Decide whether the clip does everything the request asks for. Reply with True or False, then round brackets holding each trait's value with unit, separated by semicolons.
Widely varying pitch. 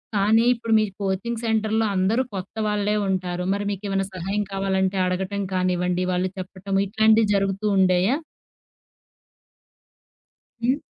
False (2.6 semitones)